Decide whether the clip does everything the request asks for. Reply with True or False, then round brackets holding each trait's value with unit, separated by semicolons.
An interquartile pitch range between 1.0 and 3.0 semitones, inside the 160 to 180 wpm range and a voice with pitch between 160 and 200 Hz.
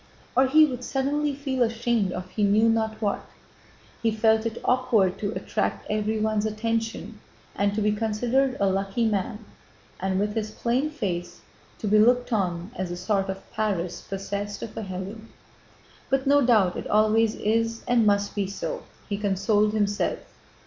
False (2.6 semitones; 165 wpm; 215 Hz)